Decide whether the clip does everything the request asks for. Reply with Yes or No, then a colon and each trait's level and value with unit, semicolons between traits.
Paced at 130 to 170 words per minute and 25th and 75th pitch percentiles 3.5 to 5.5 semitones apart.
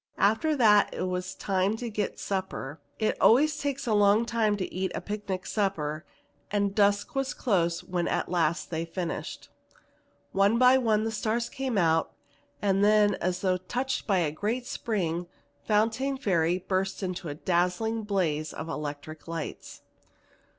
Yes: average, 155 wpm; average, 4.0 semitones